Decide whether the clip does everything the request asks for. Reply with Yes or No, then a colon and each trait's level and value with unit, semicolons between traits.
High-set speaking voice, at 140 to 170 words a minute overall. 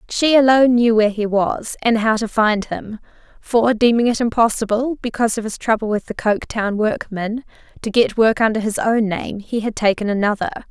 No: high, 220 Hz; average, 190 wpm